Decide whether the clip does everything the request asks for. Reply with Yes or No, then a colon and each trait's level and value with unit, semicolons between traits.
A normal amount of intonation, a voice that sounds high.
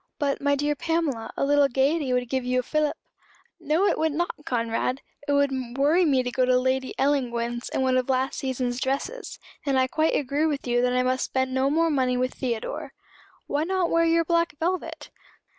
Yes: average, 3.5 semitones; very high, 275 Hz